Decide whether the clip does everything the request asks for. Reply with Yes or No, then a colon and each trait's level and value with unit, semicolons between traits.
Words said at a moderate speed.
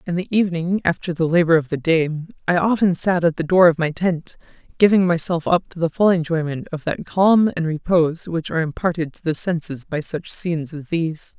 No: fast, 215 wpm